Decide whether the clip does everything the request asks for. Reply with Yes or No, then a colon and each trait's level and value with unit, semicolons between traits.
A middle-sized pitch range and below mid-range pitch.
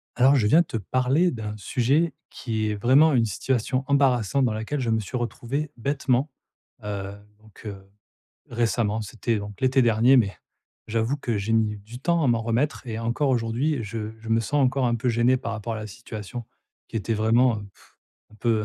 Yes: average, 3.1 semitones; low, 115 Hz